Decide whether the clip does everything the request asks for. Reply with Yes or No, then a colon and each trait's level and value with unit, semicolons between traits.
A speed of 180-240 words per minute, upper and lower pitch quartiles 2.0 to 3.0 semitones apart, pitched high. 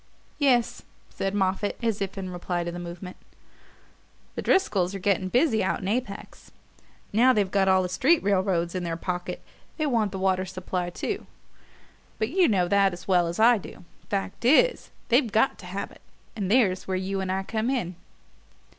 No: average, 185 wpm; average, 3.4 semitones; high, 195 Hz